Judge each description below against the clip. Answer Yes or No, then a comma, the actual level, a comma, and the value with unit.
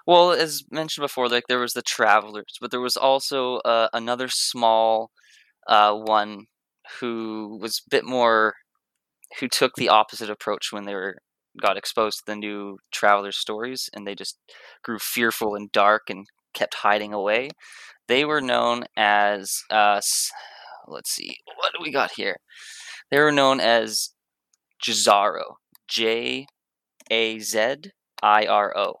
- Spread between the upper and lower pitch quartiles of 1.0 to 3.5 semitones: Yes, average, 3.1 semitones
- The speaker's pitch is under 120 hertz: Yes, low, 110 Hz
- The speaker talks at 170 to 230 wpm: No, average, 150 wpm